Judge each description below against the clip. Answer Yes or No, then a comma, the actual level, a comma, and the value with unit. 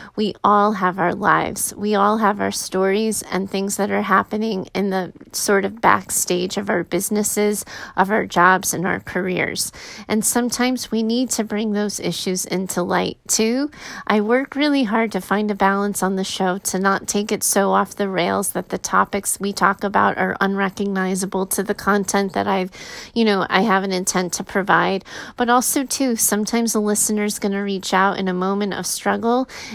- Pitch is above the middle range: Yes, high, 200 Hz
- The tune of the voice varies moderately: No, narrow, 2.2 semitones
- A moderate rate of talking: Yes, average, 190 wpm